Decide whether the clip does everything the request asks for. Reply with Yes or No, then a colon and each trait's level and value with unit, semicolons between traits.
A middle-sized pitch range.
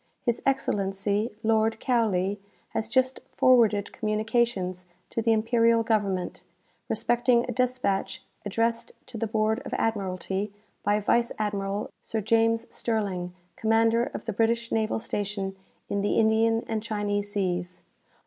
No: narrow, 2.2 semitones